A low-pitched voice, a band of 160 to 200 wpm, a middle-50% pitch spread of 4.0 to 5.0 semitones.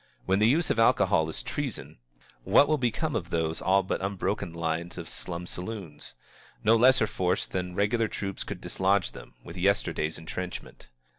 Yes: very low, 95 Hz; average, 165 wpm; average, 4.6 semitones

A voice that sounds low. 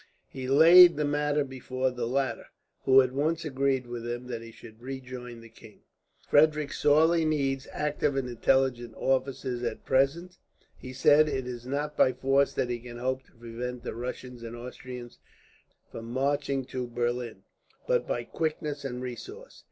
Yes: low, 130 Hz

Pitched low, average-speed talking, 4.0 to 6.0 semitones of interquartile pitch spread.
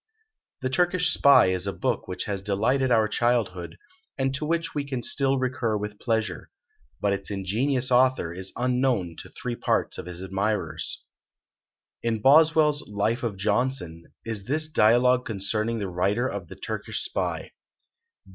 Yes: low, 115 Hz; average, 155 wpm; average, 4.8 semitones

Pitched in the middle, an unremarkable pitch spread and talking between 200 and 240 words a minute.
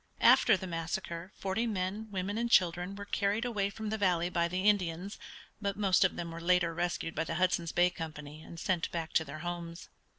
Yes: medium, 180 Hz; average, 3.0 semitones; fast, 205 wpm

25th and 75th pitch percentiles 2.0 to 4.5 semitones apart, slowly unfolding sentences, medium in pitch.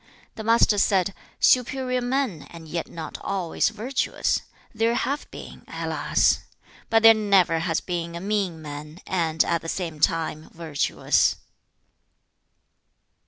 No: wide, 5.4 semitones; slow, 125 wpm; medium, 180 Hz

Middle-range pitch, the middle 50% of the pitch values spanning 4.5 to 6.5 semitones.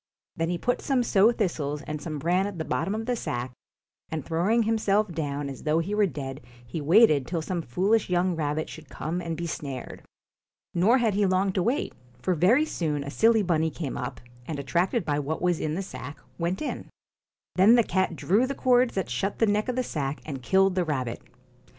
Yes: medium, 175 Hz; wide, 5.4 semitones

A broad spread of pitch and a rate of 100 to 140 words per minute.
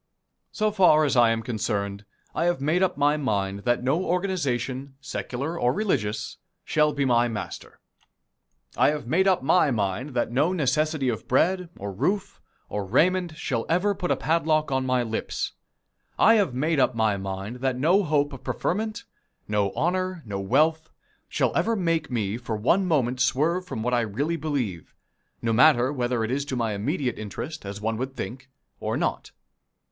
No: wide, 6.1 semitones; average, 175 wpm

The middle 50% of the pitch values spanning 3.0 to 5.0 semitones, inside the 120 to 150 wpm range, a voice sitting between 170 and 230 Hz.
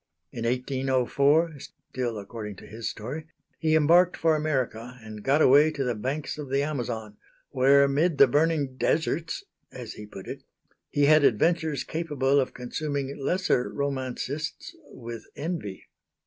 No: average, 3.9 semitones; average, 145 wpm; medium, 140 Hz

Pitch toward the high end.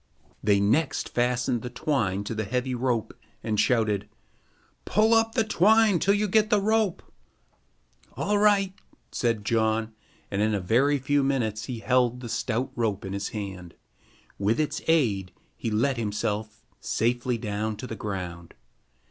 No: low, 120 Hz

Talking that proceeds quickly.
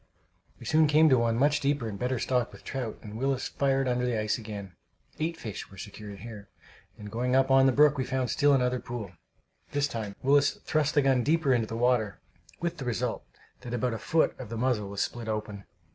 Yes: fast, 220 wpm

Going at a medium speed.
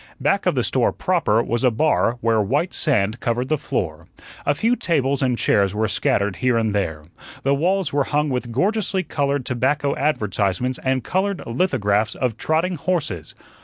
Yes: average, 170 wpm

